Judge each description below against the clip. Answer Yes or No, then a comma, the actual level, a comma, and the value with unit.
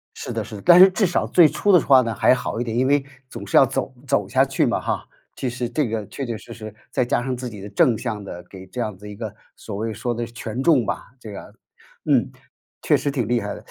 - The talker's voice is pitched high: No, low, 120 Hz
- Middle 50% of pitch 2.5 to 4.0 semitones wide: Yes, average, 3.6 semitones